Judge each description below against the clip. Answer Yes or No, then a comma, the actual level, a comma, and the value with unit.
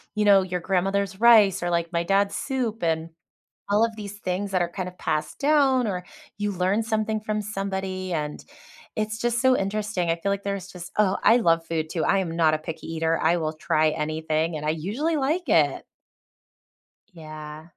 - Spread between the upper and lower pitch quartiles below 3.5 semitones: No, average, 4.4 semitones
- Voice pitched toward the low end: No, high, 190 Hz